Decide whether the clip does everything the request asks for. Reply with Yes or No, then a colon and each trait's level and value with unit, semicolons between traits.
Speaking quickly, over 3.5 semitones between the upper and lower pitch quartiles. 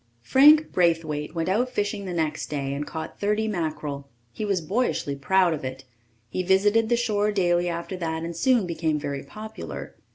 No: average, 175 wpm; average, 5.1 semitones